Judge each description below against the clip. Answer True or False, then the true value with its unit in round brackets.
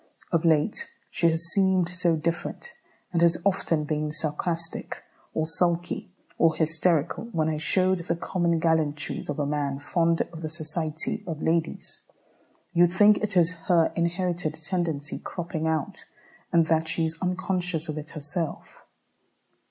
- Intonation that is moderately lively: False (1.9 semitones)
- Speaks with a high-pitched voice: False (165 Hz)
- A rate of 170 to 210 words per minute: False (145 wpm)